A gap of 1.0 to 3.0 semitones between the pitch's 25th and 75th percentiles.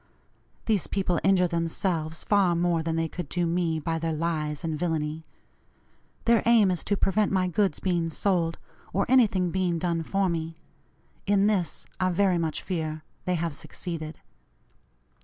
Yes: average, 2.7 semitones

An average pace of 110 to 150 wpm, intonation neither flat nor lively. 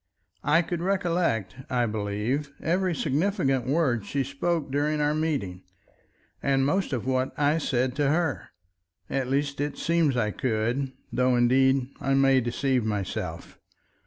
Yes: average, 140 wpm; average, 3.5 semitones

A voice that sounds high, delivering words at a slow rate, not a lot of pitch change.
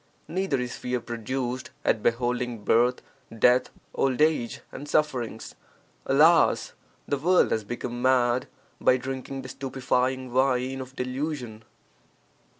No: low, 125 Hz; slow, 120 wpm; narrow, 1.8 semitones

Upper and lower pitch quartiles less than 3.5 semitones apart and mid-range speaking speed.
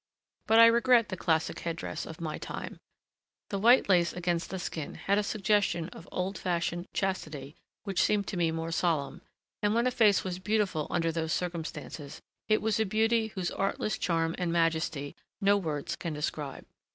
No: average, 4.0 semitones; average, 180 wpm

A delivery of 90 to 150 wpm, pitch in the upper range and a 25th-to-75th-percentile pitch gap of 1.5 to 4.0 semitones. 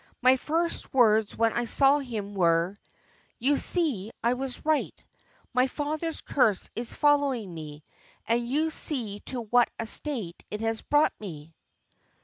No: average, 145 wpm; high, 240 Hz; wide, 5.5 semitones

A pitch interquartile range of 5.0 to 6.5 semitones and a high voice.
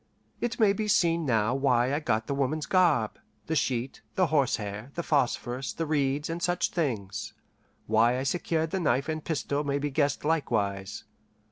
No: average, 5.3 semitones; medium, 140 Hz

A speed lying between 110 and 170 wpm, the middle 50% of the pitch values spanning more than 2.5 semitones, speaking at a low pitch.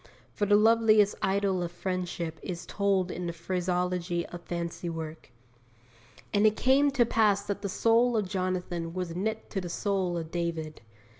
No: average, 165 wpm; average, 3.1 semitones; medium, 185 Hz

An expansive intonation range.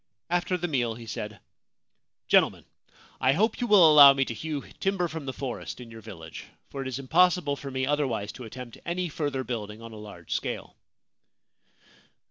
Yes: wide, 5.8 semitones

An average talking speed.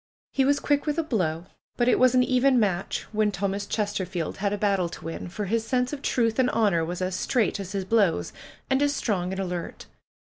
No: fast, 220 wpm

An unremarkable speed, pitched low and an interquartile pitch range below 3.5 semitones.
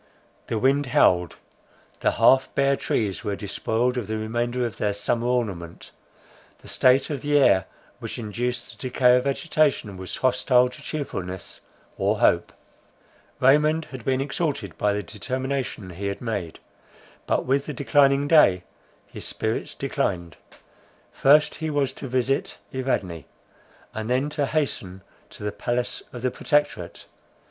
No: average, 145 wpm; low, 125 Hz; average, 5.0 semitones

